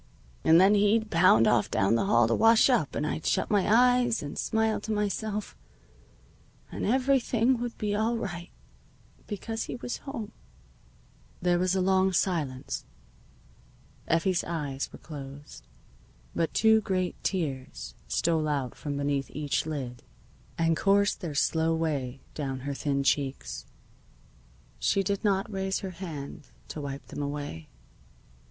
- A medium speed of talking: Yes, average, 145 wpm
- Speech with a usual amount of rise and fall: No, wide, 6.6 semitones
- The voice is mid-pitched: Yes, medium, 170 Hz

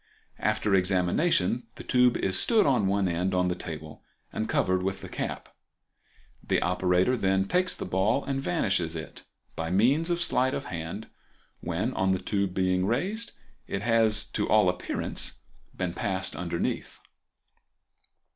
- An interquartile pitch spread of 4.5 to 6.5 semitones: Yes, average, 5.0 semitones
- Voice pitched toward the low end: Yes, very low, 95 Hz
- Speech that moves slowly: No, average, 150 wpm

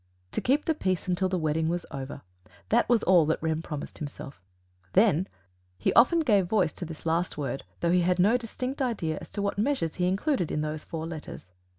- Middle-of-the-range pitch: Yes, medium, 175 Hz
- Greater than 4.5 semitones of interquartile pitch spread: Yes, average, 5.1 semitones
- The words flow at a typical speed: No, fast, 210 wpm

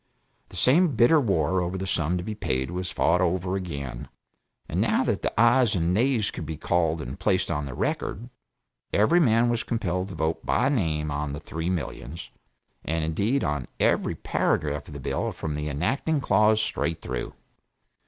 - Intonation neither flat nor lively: No, wide, 6.0 semitones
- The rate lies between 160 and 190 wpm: Yes, average, 180 wpm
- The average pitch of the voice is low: Yes, very low, 90 Hz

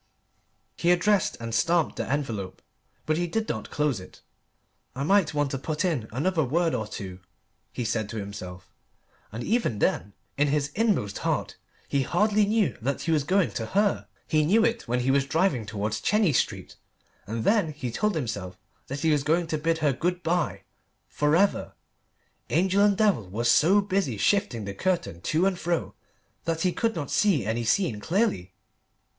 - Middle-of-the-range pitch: Yes, medium, 150 Hz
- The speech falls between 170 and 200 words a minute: Yes, average, 180 wpm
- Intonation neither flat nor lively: No, wide, 8.2 semitones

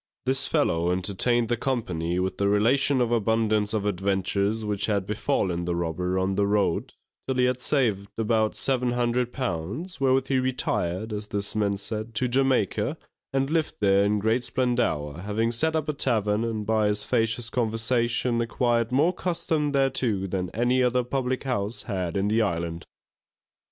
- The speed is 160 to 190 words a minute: Yes, average, 165 wpm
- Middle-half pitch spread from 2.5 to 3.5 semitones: No, average, 4.1 semitones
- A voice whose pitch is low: Yes, low, 110 Hz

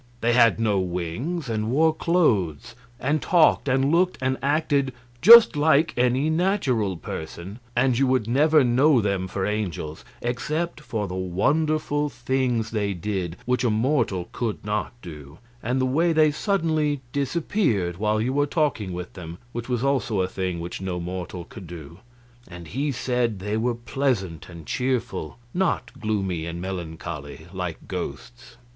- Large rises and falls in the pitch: Yes, wide, 7.2 semitones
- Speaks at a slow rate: No, average, 155 wpm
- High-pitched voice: No, low, 120 Hz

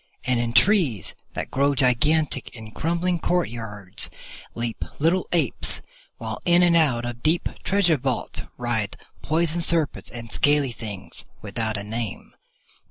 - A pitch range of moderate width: No, wide, 6.2 semitones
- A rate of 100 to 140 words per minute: Yes, slow, 135 wpm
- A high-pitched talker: No, low, 130 Hz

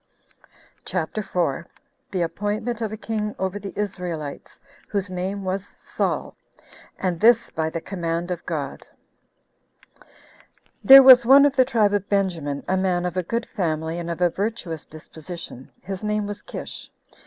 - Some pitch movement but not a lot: Yes, average, 3.9 semitones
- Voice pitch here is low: No, high, 190 Hz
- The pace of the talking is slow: No, average, 155 wpm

